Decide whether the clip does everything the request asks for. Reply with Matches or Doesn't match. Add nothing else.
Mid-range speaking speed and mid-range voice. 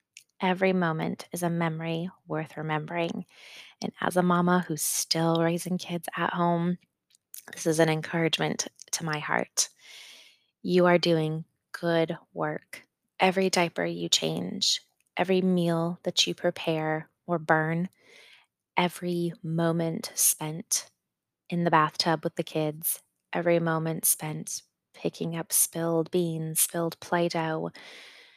Doesn't match